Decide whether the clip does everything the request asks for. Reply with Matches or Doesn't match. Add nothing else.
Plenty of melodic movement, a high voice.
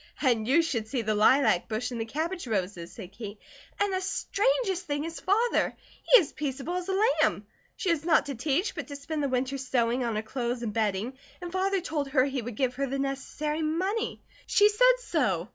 Matches